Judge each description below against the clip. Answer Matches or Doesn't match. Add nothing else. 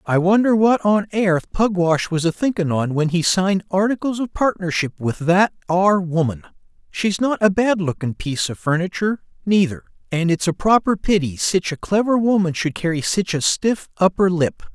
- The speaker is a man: Matches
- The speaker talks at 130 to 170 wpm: Doesn't match